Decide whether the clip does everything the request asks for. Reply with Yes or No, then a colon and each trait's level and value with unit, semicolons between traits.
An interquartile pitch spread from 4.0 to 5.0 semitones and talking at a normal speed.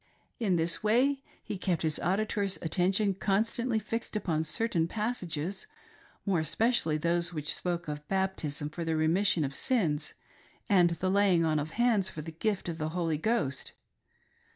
Yes: average, 4.7 semitones; average, 160 wpm